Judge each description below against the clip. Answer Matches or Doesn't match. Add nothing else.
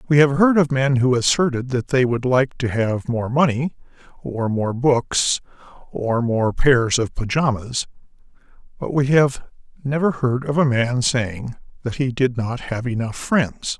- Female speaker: Doesn't match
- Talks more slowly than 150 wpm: Doesn't match